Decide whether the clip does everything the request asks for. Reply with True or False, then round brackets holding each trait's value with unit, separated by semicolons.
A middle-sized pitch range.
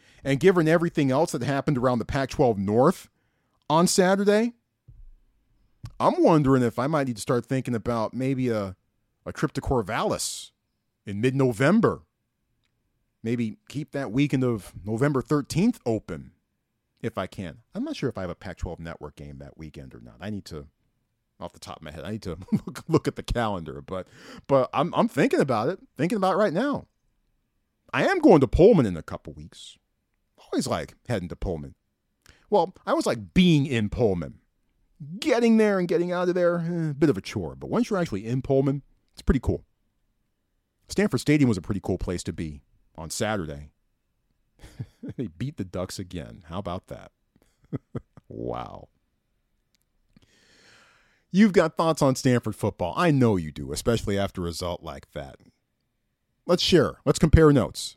False (8.3 semitones)